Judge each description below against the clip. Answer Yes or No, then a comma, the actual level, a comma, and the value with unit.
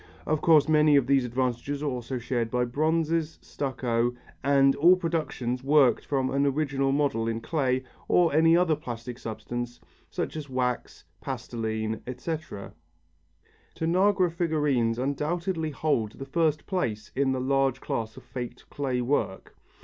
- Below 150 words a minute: Yes, average, 140 wpm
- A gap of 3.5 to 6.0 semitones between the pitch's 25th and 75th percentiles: Yes, average, 4.2 semitones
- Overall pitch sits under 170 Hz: Yes, low, 135 Hz